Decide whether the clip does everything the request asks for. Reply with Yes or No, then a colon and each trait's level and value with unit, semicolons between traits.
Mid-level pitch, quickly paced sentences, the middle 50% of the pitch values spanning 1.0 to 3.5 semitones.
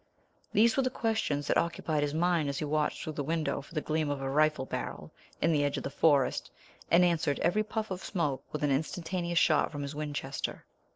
Yes: medium, 155 Hz; fast, 220 wpm; average, 3.0 semitones